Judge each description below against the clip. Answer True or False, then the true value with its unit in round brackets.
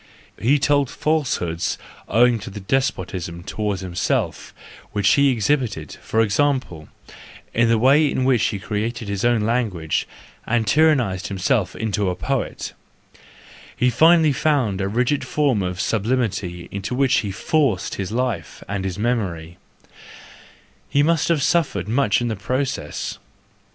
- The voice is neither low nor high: False (110 Hz)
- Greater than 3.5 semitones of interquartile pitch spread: True (5.6 semitones)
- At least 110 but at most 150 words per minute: True (135 wpm)